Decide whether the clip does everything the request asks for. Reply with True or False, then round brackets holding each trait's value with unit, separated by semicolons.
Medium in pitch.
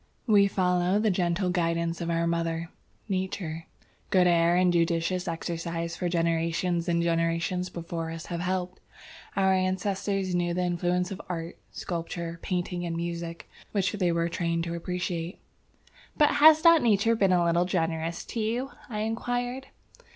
True (175 Hz)